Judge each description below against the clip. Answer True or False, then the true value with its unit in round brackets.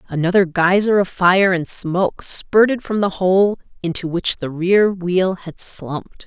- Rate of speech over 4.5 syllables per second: False (4.1 syllables/s)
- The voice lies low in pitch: False (185 Hz)